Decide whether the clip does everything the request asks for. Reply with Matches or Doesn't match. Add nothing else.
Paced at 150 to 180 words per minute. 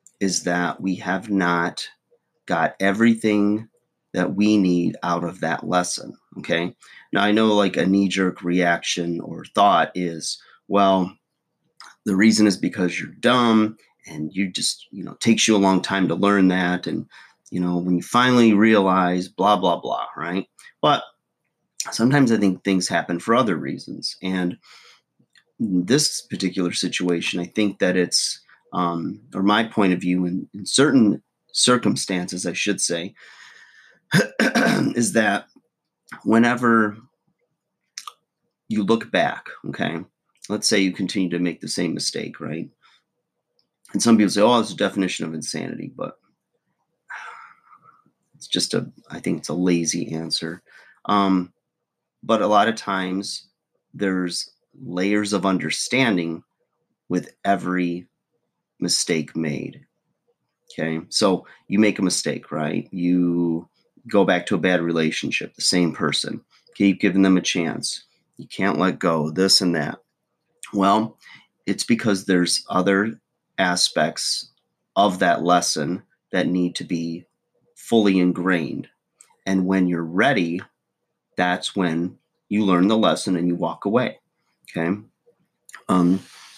Doesn't match